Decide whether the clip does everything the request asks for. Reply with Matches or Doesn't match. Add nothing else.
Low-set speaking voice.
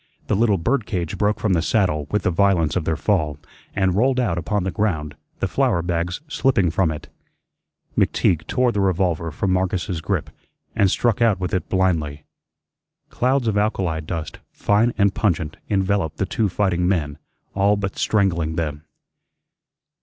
Matches